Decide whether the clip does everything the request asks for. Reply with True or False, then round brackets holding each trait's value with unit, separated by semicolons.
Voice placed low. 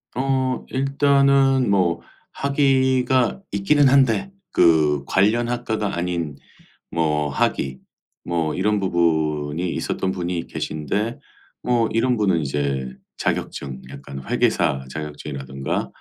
True (95 Hz)